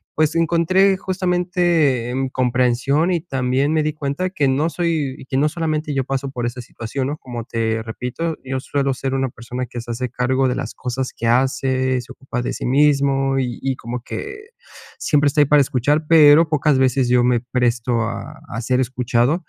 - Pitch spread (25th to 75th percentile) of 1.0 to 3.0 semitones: No, average, 3.5 semitones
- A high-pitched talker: No, low, 135 Hz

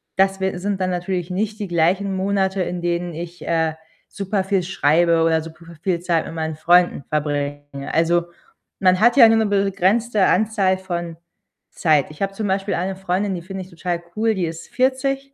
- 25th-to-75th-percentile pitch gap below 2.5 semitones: No, average, 2.8 semitones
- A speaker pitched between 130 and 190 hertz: Yes, medium, 185 Hz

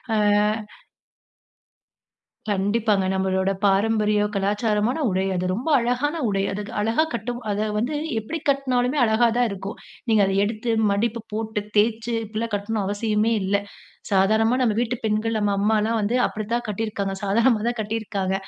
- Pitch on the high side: Yes, high, 215 Hz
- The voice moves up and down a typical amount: No, narrow, 2.3 semitones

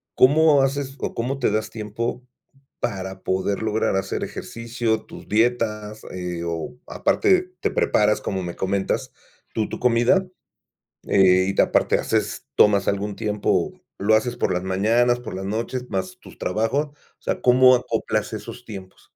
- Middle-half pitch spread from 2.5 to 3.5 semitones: No, average, 4.2 semitones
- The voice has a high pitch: No, low, 110 Hz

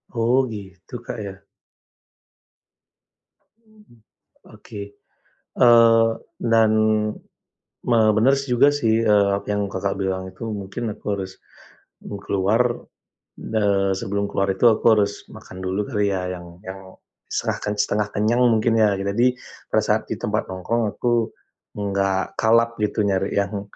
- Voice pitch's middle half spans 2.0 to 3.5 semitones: Yes, average, 3.0 semitones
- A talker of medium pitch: No, low, 105 Hz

